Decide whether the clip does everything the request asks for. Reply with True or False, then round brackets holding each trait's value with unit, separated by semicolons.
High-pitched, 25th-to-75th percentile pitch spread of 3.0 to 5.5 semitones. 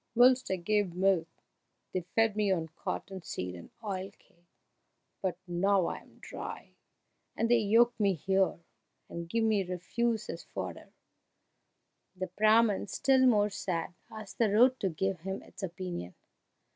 True (195 Hz; 3.6 semitones)